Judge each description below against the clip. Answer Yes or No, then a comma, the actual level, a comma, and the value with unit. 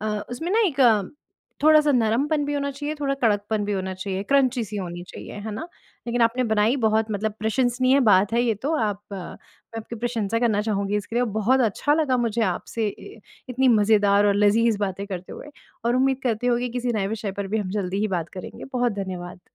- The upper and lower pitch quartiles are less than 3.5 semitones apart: No, average, 3.8 semitones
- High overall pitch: Yes, high, 225 Hz